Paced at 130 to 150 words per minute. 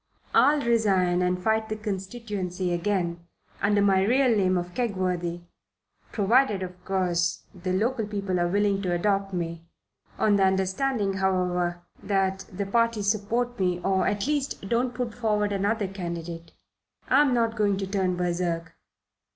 Yes: average, 145 wpm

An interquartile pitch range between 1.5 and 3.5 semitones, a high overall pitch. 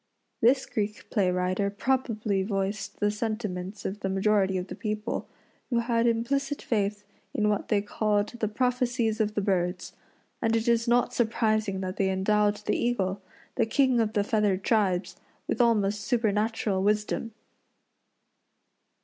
Yes: narrow, 2.6 semitones; high, 210 Hz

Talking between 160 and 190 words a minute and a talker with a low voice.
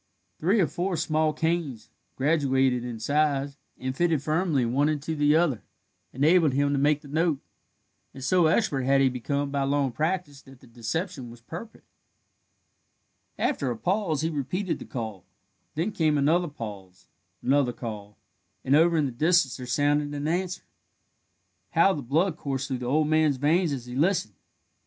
No: average, 165 wpm; medium, 145 Hz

